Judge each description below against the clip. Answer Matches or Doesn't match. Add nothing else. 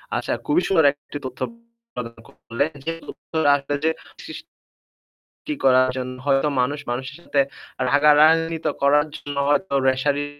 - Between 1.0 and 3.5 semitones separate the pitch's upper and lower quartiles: Matches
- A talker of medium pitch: Matches